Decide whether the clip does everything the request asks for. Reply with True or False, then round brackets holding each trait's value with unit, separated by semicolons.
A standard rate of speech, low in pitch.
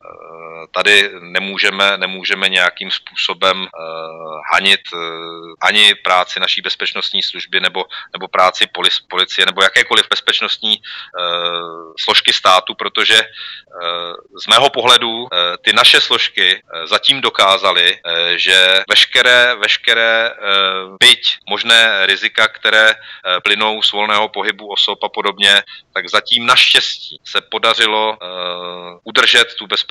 True (125 wpm; 95 Hz)